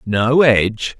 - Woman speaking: No, male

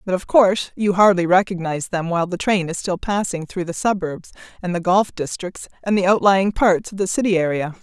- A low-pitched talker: No, medium, 185 Hz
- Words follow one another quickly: Yes, fast, 215 wpm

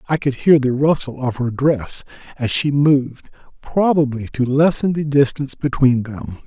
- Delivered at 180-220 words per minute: No, average, 165 wpm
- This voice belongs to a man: Yes, male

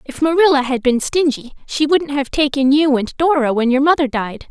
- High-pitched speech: Yes, very high, 280 Hz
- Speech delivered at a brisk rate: Yes, fast, 215 wpm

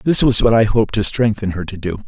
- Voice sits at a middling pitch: No, low, 110 Hz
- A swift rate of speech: Yes, fast, 290 wpm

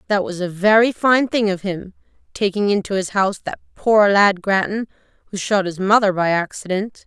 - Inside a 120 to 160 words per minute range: No, average, 180 wpm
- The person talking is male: No, female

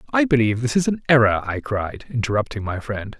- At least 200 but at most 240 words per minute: Yes, fast, 205 wpm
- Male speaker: Yes, male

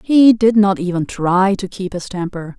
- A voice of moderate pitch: No, high, 195 Hz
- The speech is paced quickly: Yes, fast, 210 wpm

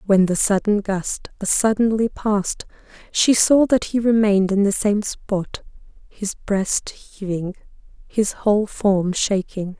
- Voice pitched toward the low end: No, high, 205 Hz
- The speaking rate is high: No, average, 140 wpm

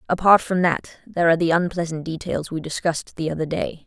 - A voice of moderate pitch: Yes, medium, 170 Hz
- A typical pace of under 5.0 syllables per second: No, 6.1 syllables/s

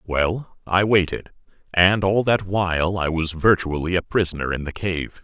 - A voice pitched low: Yes, very low, 90 Hz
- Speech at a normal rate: Yes, average, 170 wpm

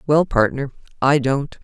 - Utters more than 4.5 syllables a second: No, 4.2 syllables/s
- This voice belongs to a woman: Yes, female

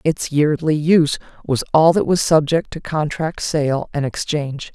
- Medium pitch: Yes, medium, 155 Hz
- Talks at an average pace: Yes, average, 165 wpm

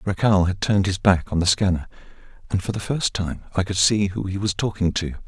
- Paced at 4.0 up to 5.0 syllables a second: No, 5.7 syllables/s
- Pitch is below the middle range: Yes, very low, 95 Hz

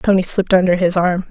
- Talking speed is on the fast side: Yes, fast, 230 wpm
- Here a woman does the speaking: Yes, female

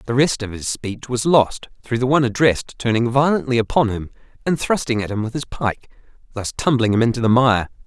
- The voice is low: Yes, low, 120 Hz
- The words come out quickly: Yes, fast, 215 wpm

